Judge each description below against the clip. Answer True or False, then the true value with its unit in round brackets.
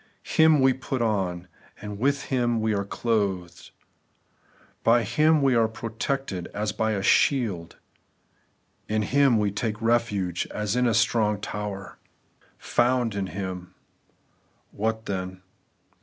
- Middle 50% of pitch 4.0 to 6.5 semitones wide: False (3.2 semitones)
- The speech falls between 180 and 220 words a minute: False (135 wpm)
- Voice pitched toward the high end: False (110 Hz)